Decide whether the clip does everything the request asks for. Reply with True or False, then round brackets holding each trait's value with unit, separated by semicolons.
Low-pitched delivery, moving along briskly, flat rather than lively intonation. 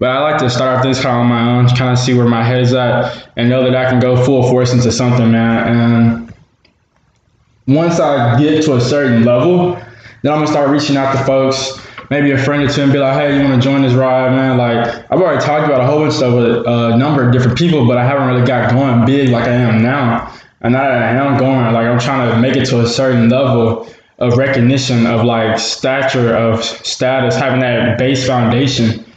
True (125 Hz; 240 wpm; 2.3 semitones)